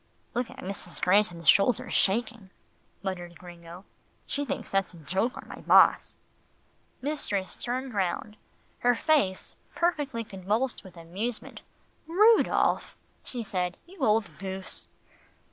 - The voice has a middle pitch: No, high, 200 Hz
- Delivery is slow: Yes, slow, 120 wpm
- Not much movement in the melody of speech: No, average, 5.0 semitones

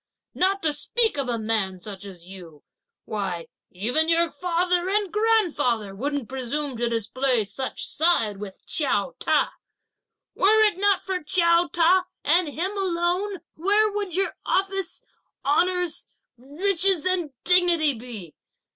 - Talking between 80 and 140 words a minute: Yes, slow, 135 wpm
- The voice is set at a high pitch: Yes, very high, 325 Hz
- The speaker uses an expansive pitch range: Yes, wide, 8.0 semitones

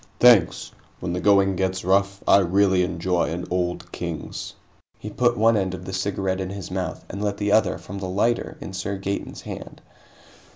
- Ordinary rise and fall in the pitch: No, narrow, 1.6 semitones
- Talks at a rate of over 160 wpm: Yes, average, 190 wpm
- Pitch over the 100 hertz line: No, very low, 95 Hz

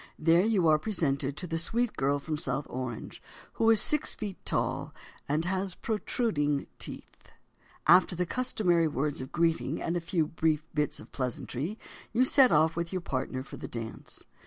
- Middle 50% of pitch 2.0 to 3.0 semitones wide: No, average, 4.9 semitones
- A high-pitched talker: No, medium, 165 Hz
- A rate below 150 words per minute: No, average, 175 wpm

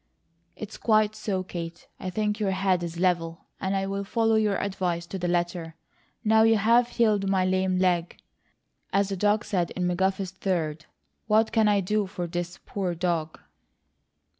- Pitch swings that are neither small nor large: Yes, average, 3.0 semitones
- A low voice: No, high, 190 Hz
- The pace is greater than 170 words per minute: No, average, 165 wpm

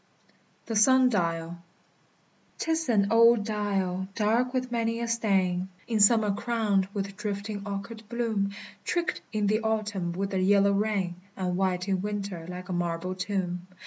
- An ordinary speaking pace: Yes, average, 155 wpm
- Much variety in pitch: No, average, 3.2 semitones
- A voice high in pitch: Yes, high, 200 Hz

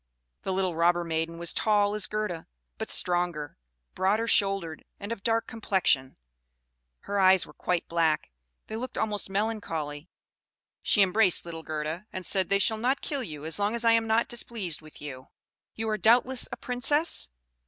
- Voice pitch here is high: Yes, high, 195 Hz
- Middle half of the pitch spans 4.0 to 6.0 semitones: Yes, average, 5.0 semitones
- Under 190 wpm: Yes, average, 175 wpm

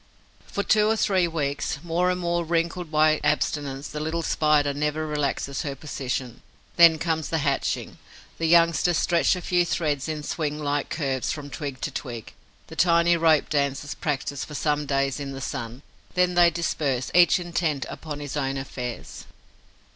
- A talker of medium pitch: Yes, medium, 150 Hz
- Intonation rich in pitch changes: No, average, 3.2 semitones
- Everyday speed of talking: Yes, average, 170 wpm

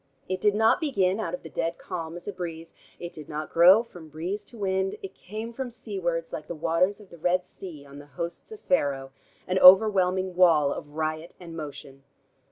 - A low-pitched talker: No, medium, 180 Hz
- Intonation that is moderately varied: Yes, average, 3.4 semitones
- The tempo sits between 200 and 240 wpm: Yes, fast, 205 wpm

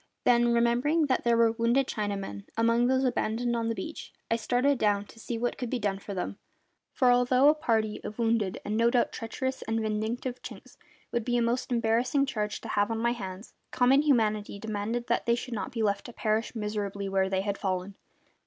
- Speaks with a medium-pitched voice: No, high, 230 Hz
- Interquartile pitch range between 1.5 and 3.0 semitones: Yes, average, 2.7 semitones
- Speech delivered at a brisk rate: Yes, fast, 210 wpm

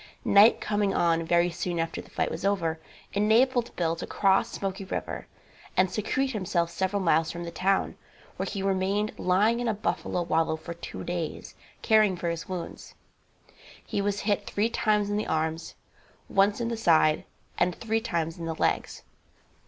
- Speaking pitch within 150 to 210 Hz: Yes, high, 190 Hz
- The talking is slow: No, average, 175 wpm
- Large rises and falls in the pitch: No, average, 3.7 semitones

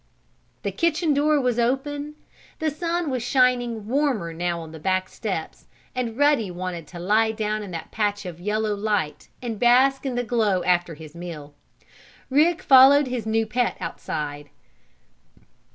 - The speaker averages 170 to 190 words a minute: No, average, 155 wpm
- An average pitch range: No, wide, 6.8 semitones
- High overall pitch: Yes, high, 220 Hz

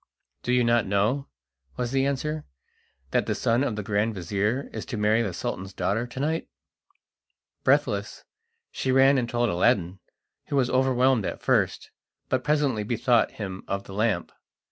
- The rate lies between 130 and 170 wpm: Yes, average, 165 wpm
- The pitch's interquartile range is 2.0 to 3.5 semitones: No, average, 4.3 semitones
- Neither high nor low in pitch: No, low, 120 Hz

